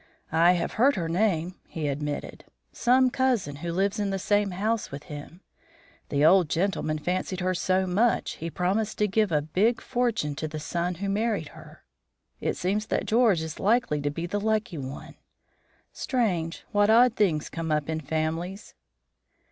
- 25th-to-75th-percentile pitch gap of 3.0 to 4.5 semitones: No, average, 5.0 semitones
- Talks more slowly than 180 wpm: Yes, average, 170 wpm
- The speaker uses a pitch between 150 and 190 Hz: Yes, medium, 185 Hz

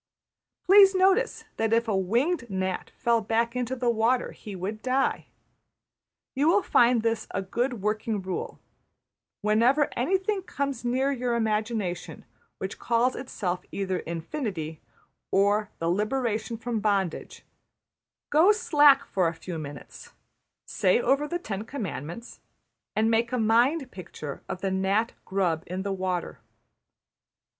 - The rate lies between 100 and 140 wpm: Yes, slow, 135 wpm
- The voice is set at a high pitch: Yes, high, 225 Hz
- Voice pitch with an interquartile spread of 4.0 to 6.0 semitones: Yes, average, 5.3 semitones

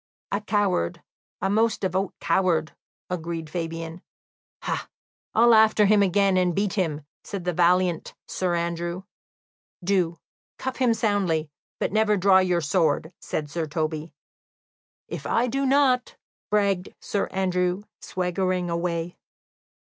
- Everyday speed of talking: No, slow, 130 wpm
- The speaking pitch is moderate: Yes, medium, 180 Hz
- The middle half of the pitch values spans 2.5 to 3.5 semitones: Yes, average, 3.2 semitones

